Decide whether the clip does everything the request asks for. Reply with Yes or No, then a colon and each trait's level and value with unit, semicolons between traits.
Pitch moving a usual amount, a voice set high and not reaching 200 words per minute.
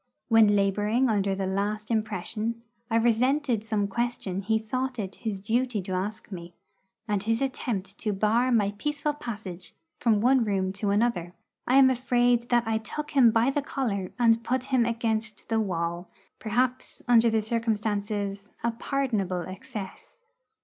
Yes: average, 3.2 semitones; high, 220 Hz; average, 155 wpm